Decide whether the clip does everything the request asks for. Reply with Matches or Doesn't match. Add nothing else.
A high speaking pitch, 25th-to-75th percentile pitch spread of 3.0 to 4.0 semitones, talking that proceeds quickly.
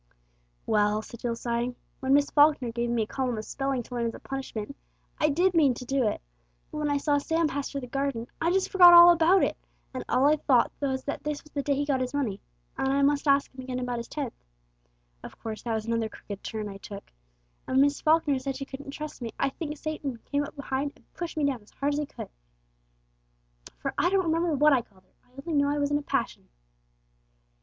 Matches